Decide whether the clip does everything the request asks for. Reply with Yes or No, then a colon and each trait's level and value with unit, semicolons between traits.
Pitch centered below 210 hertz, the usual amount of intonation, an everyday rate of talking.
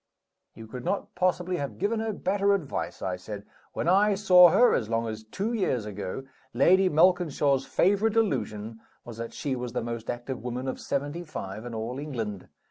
No: low, 135 Hz; wide, 8.4 semitones; average, 185 wpm